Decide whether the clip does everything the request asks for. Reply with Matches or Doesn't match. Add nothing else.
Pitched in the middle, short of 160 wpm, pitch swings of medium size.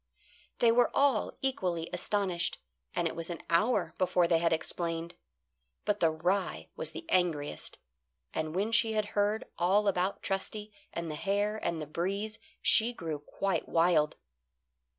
Matches